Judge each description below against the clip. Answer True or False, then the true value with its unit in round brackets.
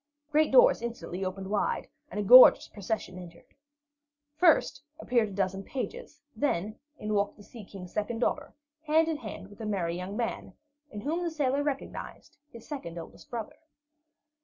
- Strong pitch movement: True (6.7 semitones)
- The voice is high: True (220 Hz)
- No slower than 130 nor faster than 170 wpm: True (165 wpm)